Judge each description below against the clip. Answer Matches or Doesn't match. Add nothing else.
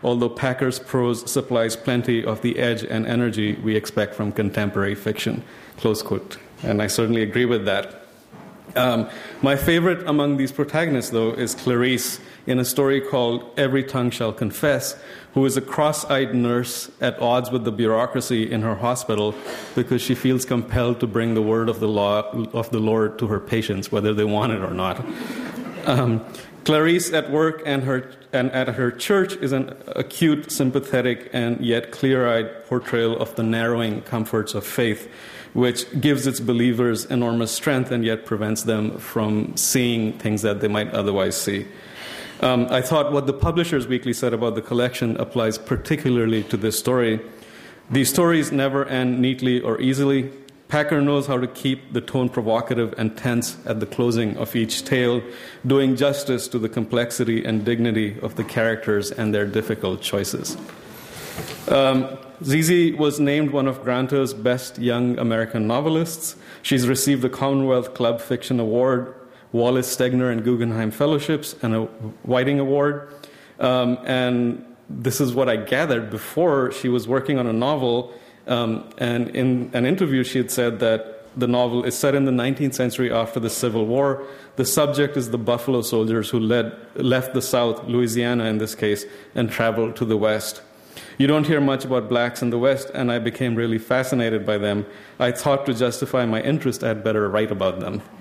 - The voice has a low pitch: Matches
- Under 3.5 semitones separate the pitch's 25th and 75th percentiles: Matches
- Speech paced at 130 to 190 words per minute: Matches